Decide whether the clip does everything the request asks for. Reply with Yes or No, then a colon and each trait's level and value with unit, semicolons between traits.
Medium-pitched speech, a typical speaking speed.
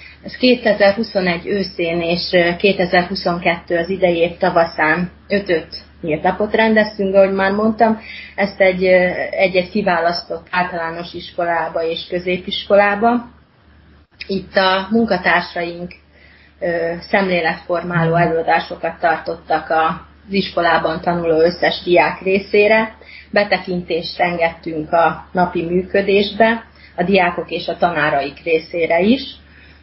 No: medium, 175 Hz; slow, 95 wpm